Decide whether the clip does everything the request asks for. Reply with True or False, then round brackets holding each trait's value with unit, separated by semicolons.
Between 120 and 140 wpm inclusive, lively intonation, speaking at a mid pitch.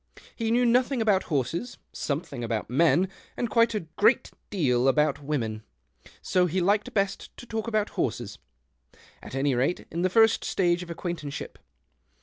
False (160 wpm; 7.4 semitones; 175 Hz)